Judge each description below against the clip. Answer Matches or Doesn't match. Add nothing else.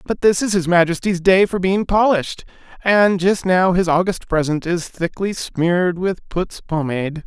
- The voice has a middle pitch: Matches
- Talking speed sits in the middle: Matches